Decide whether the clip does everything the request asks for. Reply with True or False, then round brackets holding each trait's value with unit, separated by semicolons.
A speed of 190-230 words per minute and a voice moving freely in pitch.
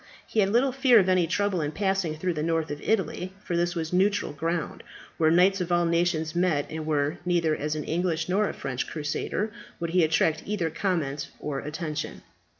False (200 wpm; 3.1 semitones)